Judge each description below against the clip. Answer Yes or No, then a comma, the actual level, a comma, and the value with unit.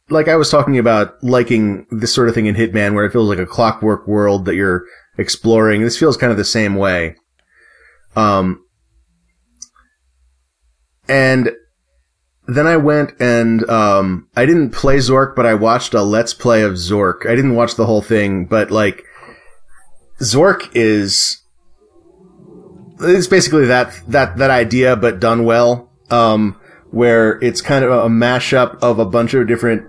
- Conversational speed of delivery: Yes, average, 160 wpm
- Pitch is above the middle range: No, low, 115 Hz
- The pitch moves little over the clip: No, average, 3.7 semitones